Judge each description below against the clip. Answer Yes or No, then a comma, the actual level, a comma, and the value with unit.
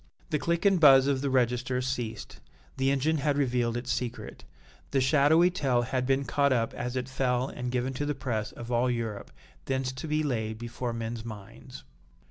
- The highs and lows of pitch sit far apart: No, narrow, 2.6 semitones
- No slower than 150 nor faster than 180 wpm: No, average, 190 wpm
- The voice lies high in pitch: No, low, 130 Hz